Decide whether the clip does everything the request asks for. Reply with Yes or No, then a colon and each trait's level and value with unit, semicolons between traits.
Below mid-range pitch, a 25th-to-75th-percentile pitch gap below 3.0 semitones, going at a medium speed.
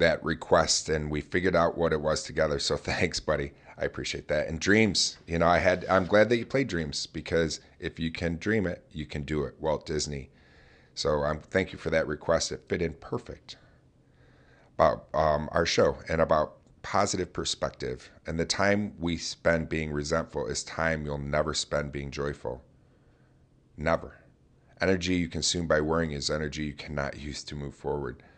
Yes: very low, 80 Hz; narrow, 2.4 semitones; average, 185 wpm